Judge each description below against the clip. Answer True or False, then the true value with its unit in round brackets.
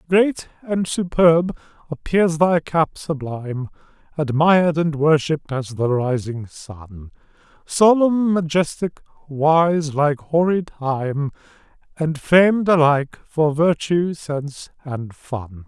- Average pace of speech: False (105 wpm)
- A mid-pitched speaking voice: True (155 Hz)